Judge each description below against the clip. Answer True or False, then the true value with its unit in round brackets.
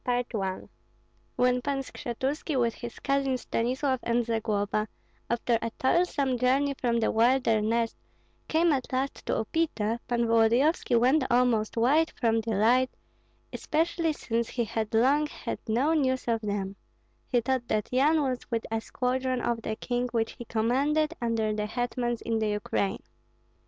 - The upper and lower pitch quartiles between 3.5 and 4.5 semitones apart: False (2.8 semitones)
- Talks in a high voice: True (240 Hz)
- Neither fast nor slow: True (150 wpm)